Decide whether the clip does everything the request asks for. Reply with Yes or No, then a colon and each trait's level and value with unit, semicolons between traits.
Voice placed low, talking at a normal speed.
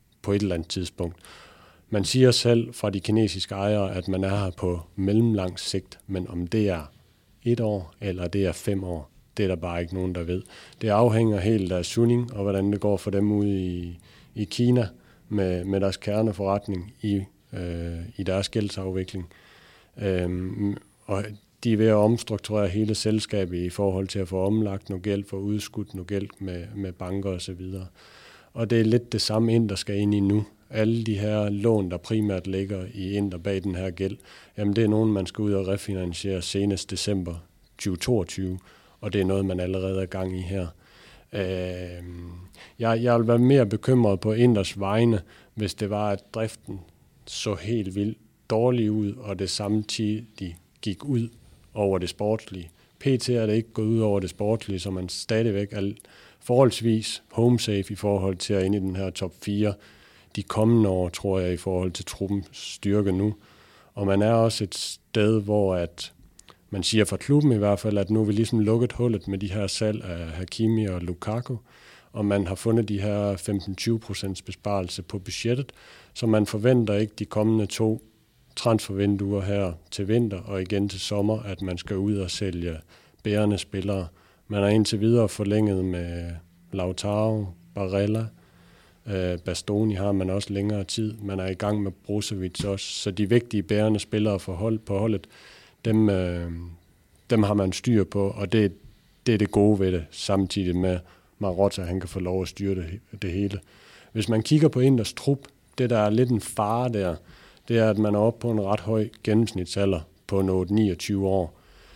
Yes: low, 100 Hz; average, 185 wpm